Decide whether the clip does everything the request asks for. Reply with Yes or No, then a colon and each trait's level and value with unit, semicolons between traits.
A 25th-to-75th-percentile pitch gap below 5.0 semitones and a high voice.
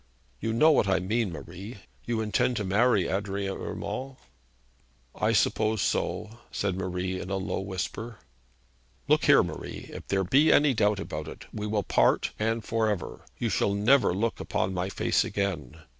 No: average, 3.1 semitones; low, 105 Hz